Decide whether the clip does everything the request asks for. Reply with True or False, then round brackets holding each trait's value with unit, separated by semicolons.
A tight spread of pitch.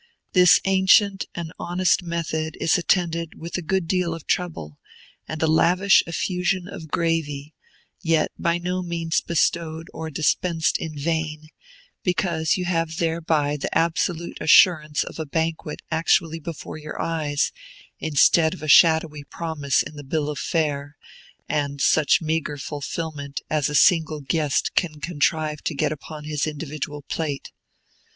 True (2.0 semitones)